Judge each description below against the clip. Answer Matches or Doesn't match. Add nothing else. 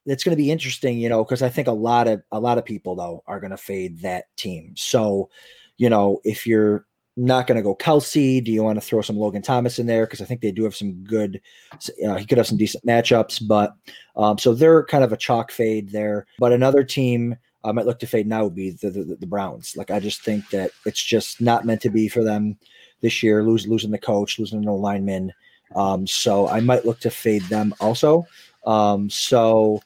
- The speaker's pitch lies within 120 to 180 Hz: Doesn't match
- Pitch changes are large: Doesn't match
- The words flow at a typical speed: Doesn't match